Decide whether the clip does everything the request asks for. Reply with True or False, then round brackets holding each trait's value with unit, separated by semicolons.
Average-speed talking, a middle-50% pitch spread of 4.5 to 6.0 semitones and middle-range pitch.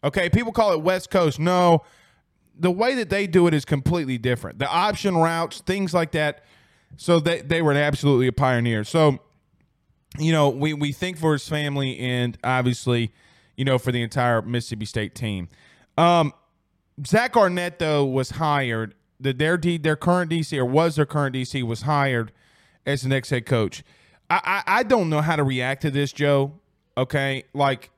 True (180 wpm; 4.8 semitones; 145 Hz)